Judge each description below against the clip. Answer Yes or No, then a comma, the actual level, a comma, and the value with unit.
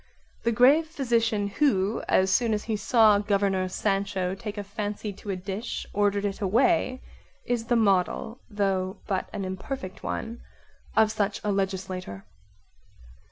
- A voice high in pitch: Yes, high, 205 Hz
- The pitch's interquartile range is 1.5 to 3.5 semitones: Yes, average, 2.8 semitones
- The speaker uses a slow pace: No, average, 145 wpm